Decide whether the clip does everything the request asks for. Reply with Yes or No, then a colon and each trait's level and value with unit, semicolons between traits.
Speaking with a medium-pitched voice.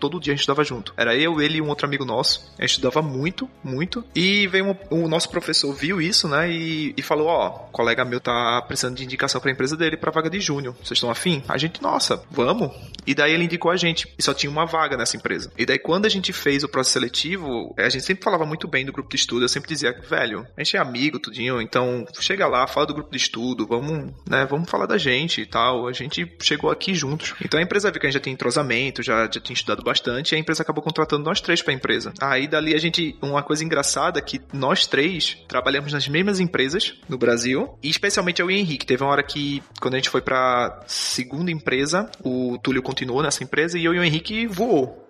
Yes: medium, 145 Hz